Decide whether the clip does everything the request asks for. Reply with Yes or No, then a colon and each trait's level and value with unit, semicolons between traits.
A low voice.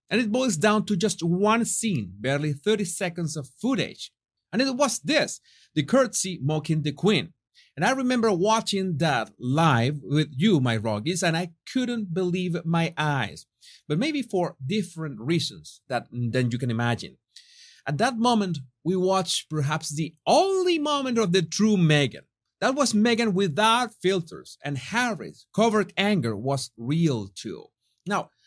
No: medium, 180 Hz